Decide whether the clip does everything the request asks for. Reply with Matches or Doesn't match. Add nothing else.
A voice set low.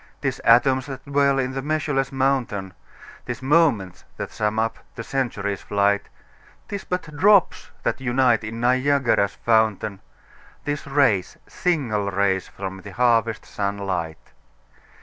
Matches